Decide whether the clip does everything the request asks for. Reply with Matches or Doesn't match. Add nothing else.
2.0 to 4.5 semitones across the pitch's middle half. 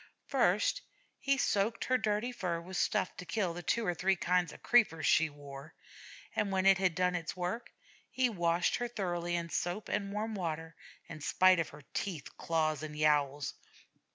Matches